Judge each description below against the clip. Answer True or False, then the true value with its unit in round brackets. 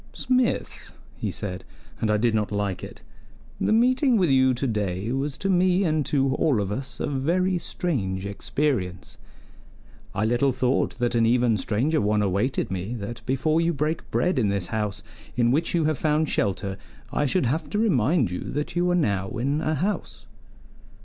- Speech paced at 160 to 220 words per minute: True (180 wpm)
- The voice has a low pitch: True (130 Hz)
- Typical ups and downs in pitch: False (7.2 semitones)